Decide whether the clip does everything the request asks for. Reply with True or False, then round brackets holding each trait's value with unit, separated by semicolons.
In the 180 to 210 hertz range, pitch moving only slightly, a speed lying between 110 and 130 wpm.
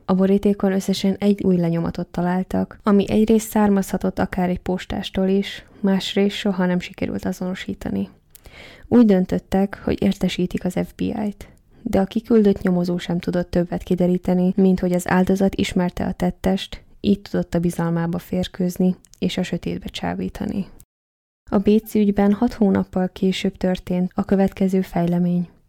False (190 Hz; 1.9 semitones; 140 wpm)